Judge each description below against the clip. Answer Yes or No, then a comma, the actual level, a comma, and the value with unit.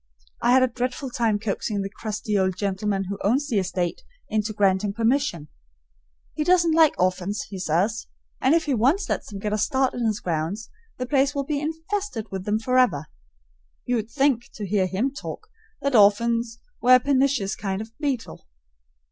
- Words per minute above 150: Yes, average, 180 wpm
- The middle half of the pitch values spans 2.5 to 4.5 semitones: No, average, 5.2 semitones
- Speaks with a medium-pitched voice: No, high, 225 Hz